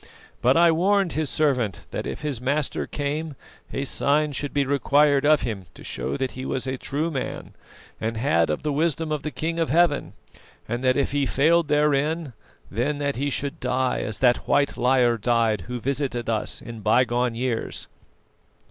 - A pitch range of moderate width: Yes, average, 3.5 semitones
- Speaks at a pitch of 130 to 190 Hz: Yes, medium, 140 Hz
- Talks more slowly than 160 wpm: No, average, 185 wpm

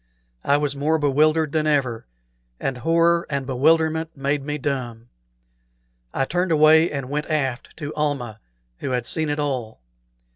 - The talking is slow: No, average, 150 wpm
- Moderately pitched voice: Yes, medium, 145 Hz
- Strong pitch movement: No, average, 2.8 semitones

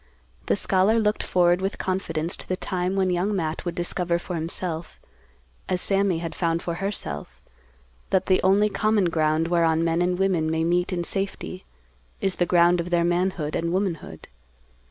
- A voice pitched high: No, medium, 175 Hz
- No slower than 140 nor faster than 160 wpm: No, average, 175 wpm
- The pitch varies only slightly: Yes, narrow, 2.1 semitones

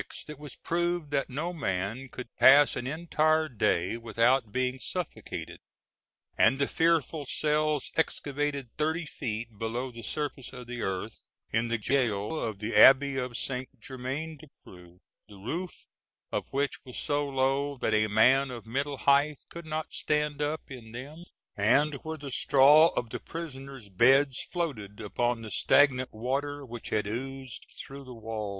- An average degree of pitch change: Yes, average, 4.3 semitones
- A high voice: No, low, 135 Hz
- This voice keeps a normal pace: Yes, average, 160 wpm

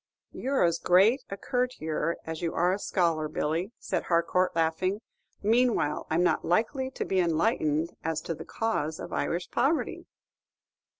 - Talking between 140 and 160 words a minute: Yes, average, 155 wpm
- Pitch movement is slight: No, average, 5.3 semitones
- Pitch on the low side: No, medium, 175 Hz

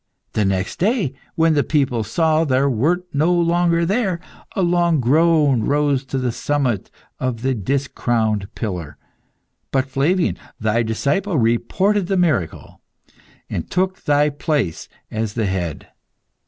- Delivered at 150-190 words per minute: No, slow, 135 wpm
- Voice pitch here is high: No, medium, 140 Hz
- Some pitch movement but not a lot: No, wide, 6.7 semitones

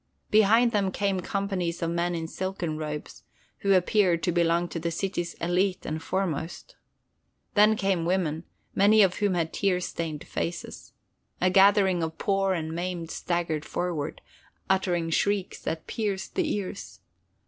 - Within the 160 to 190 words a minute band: No, average, 150 wpm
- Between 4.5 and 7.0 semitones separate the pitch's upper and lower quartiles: No, average, 2.8 semitones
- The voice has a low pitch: No, medium, 180 Hz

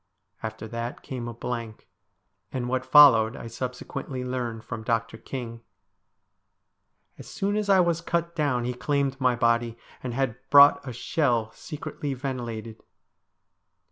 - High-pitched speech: No, low, 125 Hz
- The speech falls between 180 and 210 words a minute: No, average, 140 wpm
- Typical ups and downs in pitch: Yes, average, 3.4 semitones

